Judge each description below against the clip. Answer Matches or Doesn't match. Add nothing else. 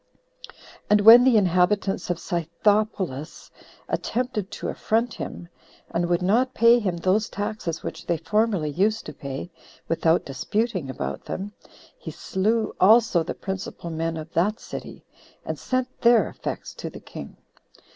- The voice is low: Doesn't match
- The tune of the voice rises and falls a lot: Doesn't match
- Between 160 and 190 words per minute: Doesn't match